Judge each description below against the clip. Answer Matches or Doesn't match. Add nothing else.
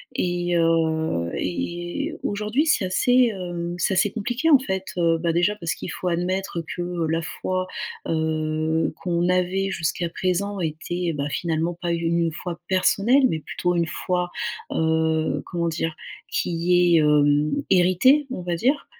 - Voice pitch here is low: Doesn't match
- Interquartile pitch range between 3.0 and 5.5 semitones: Doesn't match